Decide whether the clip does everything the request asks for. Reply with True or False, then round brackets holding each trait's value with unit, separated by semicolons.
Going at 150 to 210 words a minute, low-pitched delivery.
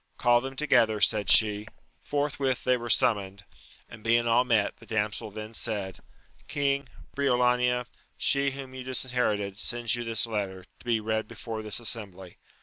True (155 wpm; 115 Hz)